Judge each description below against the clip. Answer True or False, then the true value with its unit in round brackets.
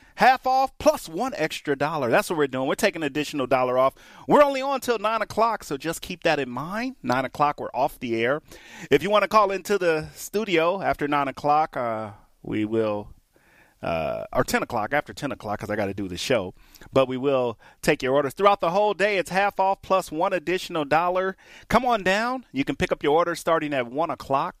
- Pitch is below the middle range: False (160 Hz)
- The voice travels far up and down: True (6.8 semitones)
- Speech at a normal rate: False (225 wpm)